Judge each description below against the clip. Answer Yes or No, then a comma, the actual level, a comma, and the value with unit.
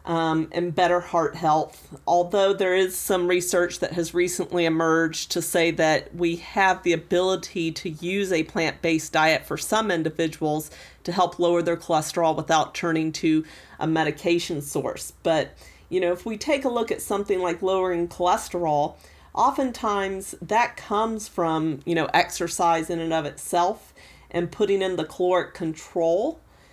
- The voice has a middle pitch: Yes, medium, 175 Hz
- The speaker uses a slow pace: No, average, 160 wpm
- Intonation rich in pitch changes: No, narrow, 2.4 semitones